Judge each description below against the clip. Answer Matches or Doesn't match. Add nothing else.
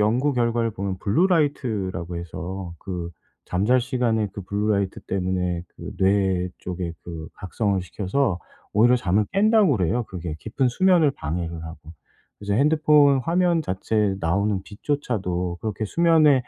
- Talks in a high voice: Doesn't match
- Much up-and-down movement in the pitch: Matches